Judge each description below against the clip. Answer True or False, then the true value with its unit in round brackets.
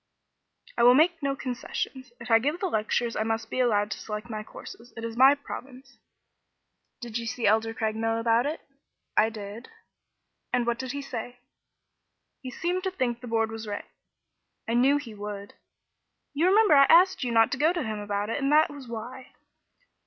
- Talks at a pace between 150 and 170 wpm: False (190 wpm)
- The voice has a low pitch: False (240 Hz)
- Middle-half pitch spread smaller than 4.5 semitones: True (3.8 semitones)